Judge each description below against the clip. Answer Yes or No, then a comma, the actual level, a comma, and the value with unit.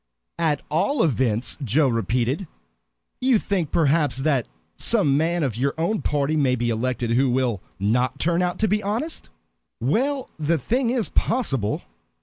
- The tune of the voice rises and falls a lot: Yes, wide, 7.4 semitones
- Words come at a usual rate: Yes, average, 150 wpm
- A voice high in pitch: No, medium, 145 Hz